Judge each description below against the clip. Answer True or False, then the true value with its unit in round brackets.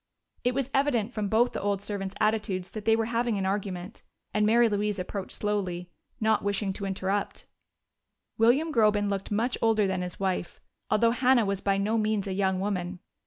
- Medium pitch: False (205 Hz)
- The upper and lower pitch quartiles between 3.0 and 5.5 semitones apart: False (2.6 semitones)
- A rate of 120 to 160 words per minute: False (185 wpm)